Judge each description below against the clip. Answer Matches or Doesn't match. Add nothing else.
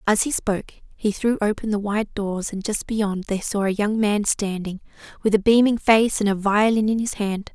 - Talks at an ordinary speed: Doesn't match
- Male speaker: Doesn't match